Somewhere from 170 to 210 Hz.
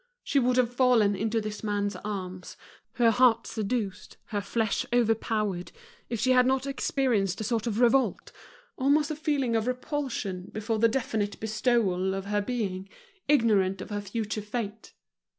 No: high, 220 Hz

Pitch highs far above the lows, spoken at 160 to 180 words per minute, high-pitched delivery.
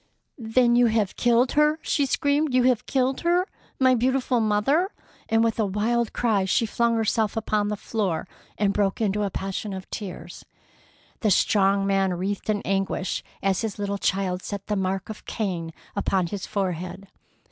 No: average, 3.6 semitones; average, 170 wpm; high, 210 Hz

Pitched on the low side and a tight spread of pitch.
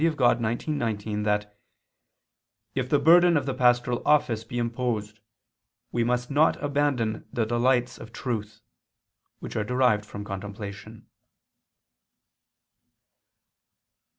No: low, 120 Hz; average, 3.5 semitones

